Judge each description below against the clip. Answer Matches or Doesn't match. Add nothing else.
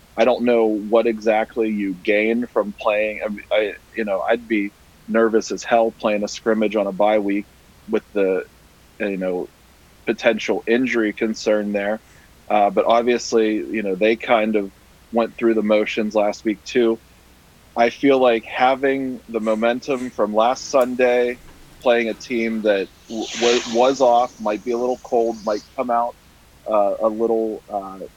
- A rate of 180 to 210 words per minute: Doesn't match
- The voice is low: Matches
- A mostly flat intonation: Matches